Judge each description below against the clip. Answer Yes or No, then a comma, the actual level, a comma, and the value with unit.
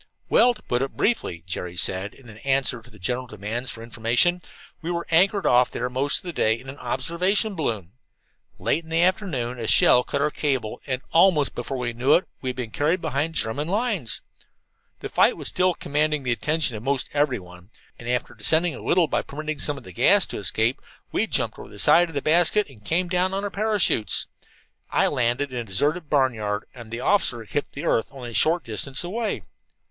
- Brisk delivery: Yes, fast, 210 wpm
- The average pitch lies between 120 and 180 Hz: Yes, low, 135 Hz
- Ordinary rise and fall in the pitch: No, wide, 6.1 semitones